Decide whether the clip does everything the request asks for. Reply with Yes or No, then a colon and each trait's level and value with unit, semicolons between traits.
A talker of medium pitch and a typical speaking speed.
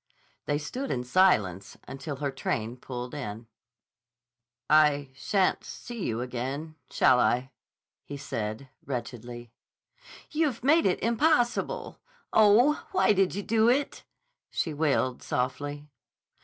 No: medium, 145 Hz; slow, 115 wpm